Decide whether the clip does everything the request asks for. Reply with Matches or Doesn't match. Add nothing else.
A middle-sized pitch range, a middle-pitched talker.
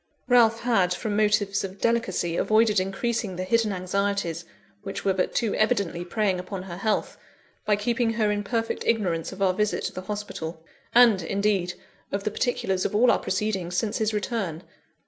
Doesn't match